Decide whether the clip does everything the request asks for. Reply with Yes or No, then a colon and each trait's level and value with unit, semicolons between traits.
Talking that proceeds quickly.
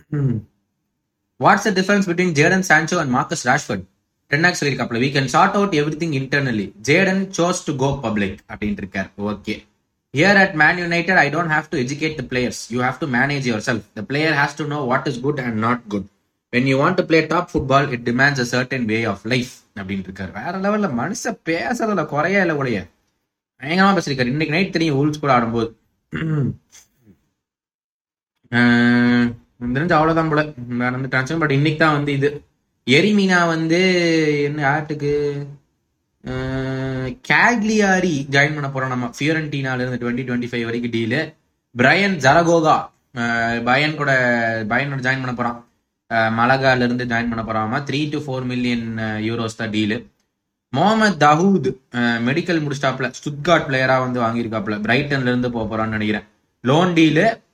Yes: fast, 135 wpm